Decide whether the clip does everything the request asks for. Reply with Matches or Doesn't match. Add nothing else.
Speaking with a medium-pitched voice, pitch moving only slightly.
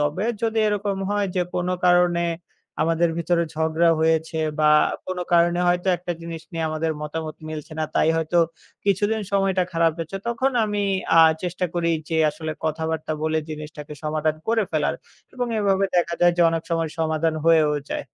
Matches